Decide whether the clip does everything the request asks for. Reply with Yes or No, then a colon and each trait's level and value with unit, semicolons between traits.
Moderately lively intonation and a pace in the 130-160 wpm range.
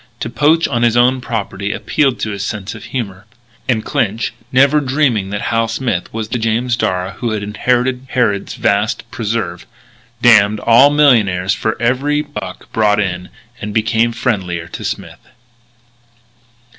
Yes: average, 3.6 semitones; average, 150 wpm